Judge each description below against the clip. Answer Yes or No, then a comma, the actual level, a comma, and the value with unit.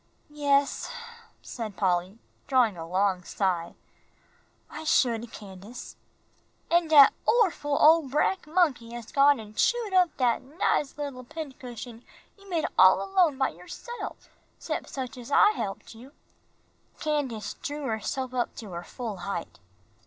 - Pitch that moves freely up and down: Yes, wide, 5.8 semitones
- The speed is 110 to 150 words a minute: Yes, average, 140 wpm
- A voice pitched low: No, very high, 255 Hz